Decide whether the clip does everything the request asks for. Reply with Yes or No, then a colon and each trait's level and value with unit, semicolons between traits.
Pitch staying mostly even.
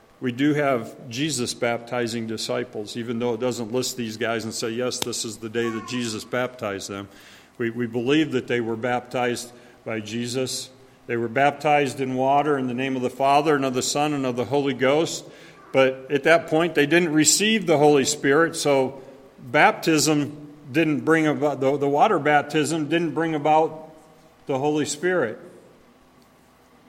No: average, 3.6 semitones